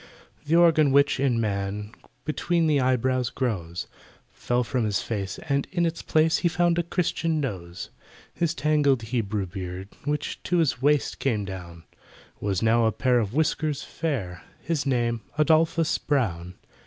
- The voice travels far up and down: Yes, wide, 7.0 semitones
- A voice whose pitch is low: Yes, low, 130 Hz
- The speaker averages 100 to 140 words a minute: No, average, 155 wpm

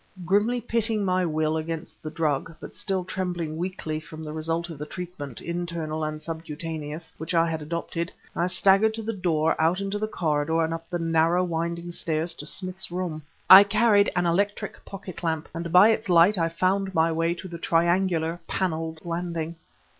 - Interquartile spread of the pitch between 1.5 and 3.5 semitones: Yes, narrow, 2.5 semitones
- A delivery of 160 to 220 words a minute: Yes, average, 185 wpm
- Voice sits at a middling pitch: Yes, medium, 170 Hz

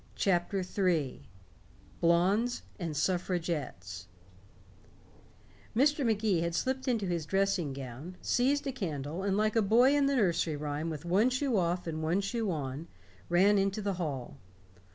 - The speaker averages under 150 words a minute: Yes, average, 140 wpm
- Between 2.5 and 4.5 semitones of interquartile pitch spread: No, average, 5.3 semitones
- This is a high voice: No, medium, 180 Hz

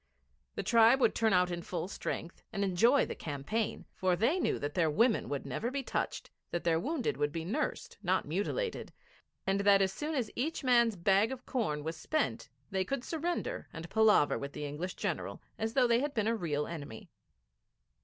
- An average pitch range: No, wide, 6.5 semitones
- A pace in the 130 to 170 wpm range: No, average, 195 wpm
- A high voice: Yes, high, 200 Hz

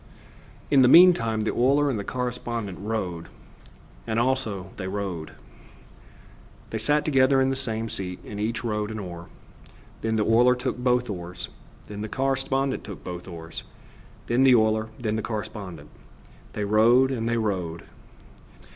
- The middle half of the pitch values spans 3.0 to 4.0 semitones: Yes, average, 3.7 semitones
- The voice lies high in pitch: No, low, 110 Hz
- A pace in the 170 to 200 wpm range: No, average, 155 wpm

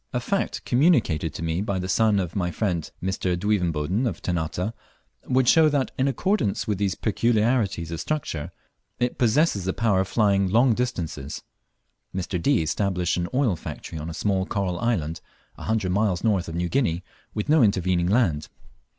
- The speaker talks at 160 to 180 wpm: Yes, average, 175 wpm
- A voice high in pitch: No, low, 100 Hz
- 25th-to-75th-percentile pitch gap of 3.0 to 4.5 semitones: No, average, 5.1 semitones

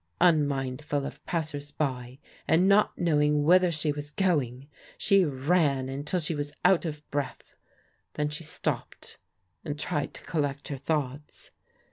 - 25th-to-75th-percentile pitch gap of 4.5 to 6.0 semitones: No, narrow, 2.5 semitones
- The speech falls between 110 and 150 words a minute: Yes, average, 140 wpm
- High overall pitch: No, medium, 150 Hz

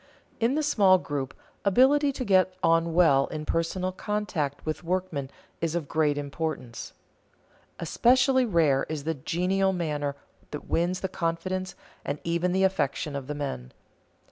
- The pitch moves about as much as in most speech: Yes, average, 4.4 semitones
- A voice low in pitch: No, medium, 170 Hz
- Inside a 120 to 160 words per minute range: Yes, average, 150 wpm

